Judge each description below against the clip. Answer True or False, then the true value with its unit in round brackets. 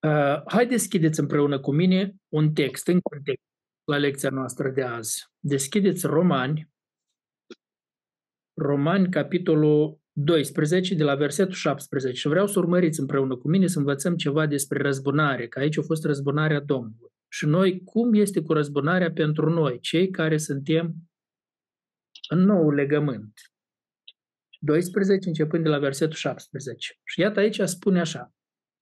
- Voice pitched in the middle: True (155 Hz)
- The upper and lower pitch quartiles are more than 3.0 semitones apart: True (3.6 semitones)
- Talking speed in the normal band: True (140 wpm)